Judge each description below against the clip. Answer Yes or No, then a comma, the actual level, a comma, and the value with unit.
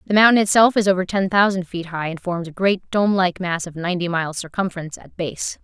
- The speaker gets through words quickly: Yes, fast, 235 wpm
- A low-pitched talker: No, medium, 185 Hz